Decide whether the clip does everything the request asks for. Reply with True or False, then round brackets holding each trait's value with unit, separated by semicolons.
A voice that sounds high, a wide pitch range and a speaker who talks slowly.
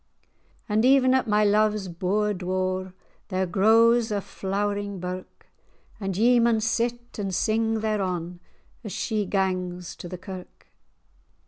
False (205 Hz; 3.1 semitones; 130 wpm)